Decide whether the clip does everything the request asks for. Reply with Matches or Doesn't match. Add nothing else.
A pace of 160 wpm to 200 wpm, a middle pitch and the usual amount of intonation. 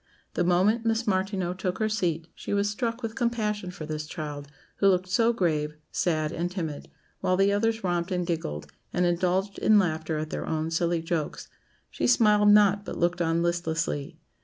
Matches